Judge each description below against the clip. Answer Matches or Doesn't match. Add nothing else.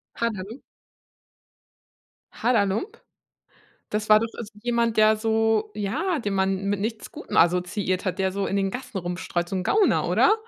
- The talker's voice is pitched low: Doesn't match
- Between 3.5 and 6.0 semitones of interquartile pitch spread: Doesn't match